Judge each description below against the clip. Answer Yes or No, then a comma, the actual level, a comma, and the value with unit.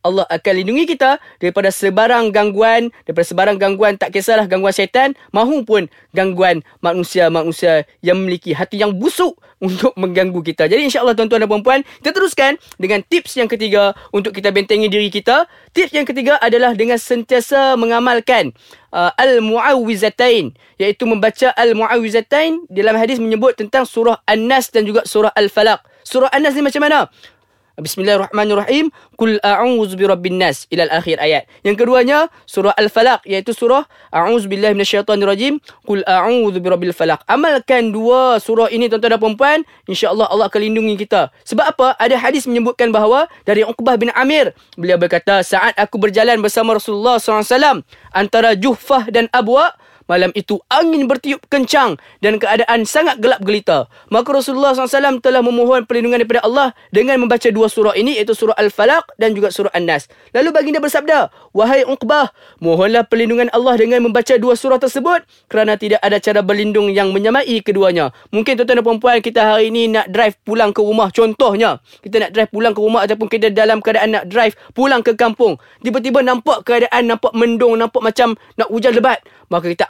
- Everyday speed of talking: No, fast, 160 wpm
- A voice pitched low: No, high, 225 Hz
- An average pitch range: Yes, average, 3.7 semitones